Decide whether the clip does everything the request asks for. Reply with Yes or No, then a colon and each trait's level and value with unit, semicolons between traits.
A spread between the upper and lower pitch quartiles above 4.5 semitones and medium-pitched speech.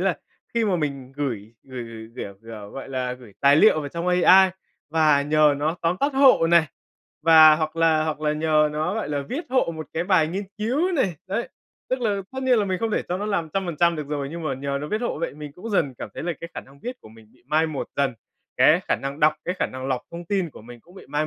Yes: average, 5.0 semitones; medium, 155 Hz